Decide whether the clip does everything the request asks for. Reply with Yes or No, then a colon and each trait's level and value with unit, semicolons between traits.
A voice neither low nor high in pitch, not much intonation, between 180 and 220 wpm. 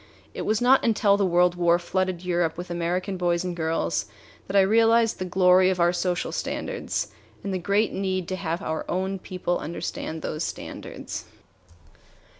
No: medium, 180 Hz; narrow, 2.0 semitones; average, 170 wpm